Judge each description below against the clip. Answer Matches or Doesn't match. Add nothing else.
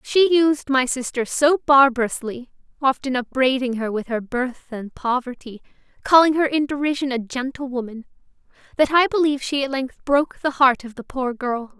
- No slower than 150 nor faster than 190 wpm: Matches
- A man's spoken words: Doesn't match